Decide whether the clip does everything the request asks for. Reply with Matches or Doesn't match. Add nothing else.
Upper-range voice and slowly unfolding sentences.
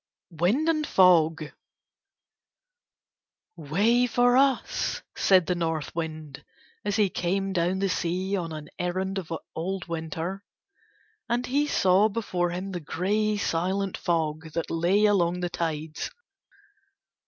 Doesn't match